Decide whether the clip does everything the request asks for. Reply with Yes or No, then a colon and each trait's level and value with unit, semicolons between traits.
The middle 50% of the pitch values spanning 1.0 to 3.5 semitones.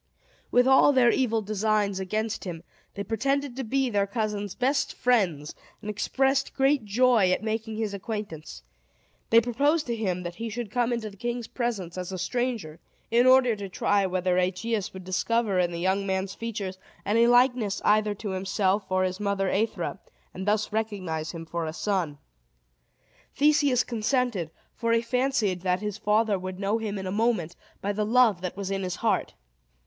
No: average, 4.0 semitones